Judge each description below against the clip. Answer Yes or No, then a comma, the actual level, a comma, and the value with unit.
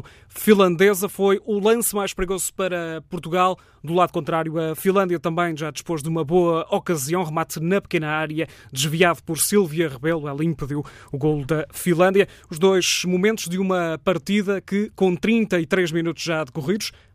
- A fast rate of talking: No, average, 160 wpm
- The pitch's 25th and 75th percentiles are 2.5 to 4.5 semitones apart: Yes, average, 3.1 semitones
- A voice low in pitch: No, medium, 175 Hz